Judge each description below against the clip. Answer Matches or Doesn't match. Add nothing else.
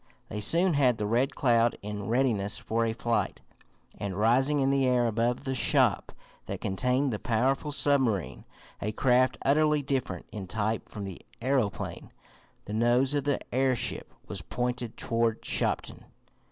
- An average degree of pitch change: Matches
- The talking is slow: Doesn't match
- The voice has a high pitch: Doesn't match